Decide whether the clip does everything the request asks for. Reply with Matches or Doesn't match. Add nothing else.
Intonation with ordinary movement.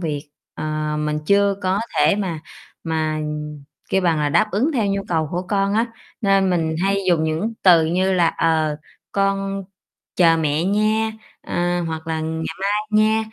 Matches